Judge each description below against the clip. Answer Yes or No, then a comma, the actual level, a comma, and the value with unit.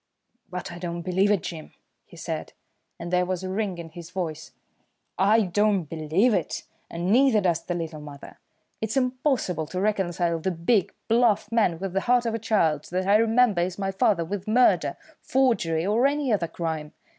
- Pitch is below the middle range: No, medium, 185 Hz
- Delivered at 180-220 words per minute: Yes, average, 185 wpm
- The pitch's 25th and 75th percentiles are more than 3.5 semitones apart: Yes, average, 4.4 semitones